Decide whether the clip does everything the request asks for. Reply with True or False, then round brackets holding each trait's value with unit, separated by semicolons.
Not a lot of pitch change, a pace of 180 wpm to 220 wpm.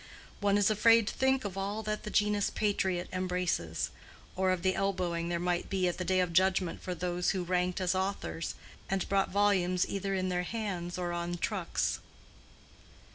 True (2.1 semitones; 185 wpm)